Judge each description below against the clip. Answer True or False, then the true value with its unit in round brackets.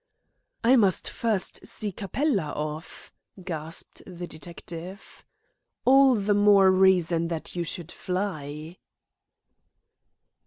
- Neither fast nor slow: False (95 wpm)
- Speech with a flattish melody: False (3.7 semitones)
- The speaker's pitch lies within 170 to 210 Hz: True (185 Hz)